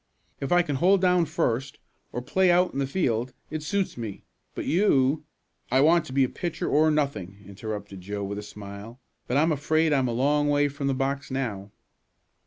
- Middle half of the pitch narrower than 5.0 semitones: No, wide, 5.5 semitones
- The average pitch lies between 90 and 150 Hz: Yes, low, 135 Hz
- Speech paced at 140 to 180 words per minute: No, average, 195 wpm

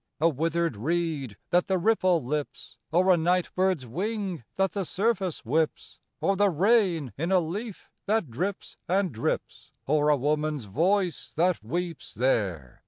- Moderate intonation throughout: Yes, average, 4.4 semitones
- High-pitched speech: No, medium, 170 Hz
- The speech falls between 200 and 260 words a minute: No, average, 155 wpm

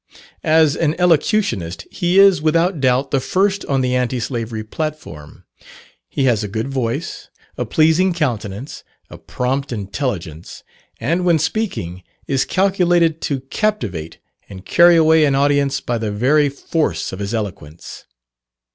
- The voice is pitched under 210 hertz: Yes, medium, 140 Hz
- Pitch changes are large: Yes, wide, 6.6 semitones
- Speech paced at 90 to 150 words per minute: Yes, average, 140 wpm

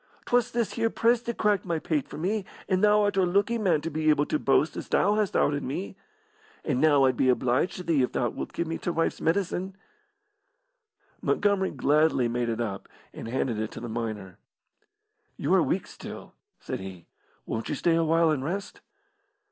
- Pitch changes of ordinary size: No, wide, 7.2 semitones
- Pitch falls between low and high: Yes, medium, 160 Hz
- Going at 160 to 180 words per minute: No, average, 195 wpm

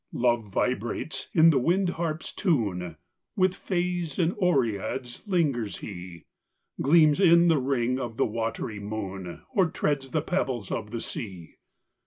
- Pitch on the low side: Yes, low, 130 Hz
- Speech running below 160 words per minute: Yes, average, 145 wpm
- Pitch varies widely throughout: Yes, wide, 7.5 semitones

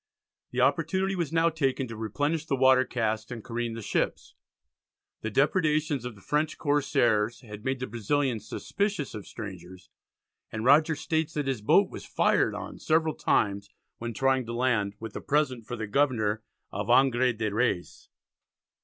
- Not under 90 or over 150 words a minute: No, average, 165 wpm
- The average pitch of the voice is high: No, low, 125 Hz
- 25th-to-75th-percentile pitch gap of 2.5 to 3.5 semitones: No, average, 5.0 semitones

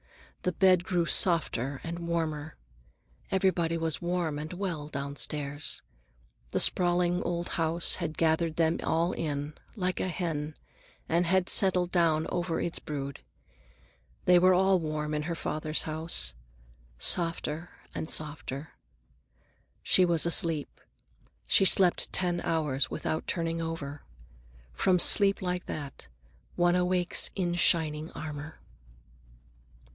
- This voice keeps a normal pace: No, slow, 120 wpm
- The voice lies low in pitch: No, medium, 165 Hz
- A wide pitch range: No, narrow, 2.6 semitones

